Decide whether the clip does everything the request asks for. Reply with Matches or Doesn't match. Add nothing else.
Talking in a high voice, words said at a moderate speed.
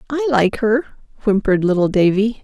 Matches